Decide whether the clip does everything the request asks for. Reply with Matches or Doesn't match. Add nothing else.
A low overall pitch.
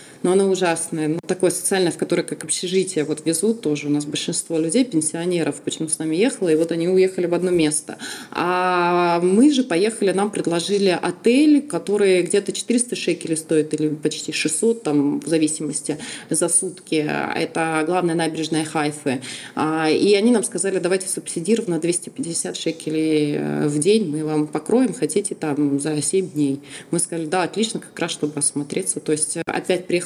Doesn't match